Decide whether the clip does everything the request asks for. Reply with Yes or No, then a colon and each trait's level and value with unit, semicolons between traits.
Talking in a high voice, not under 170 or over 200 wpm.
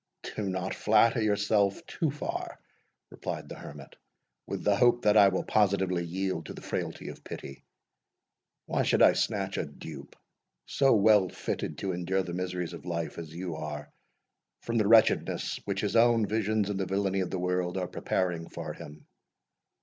No: very low, 95 Hz; average, 175 wpm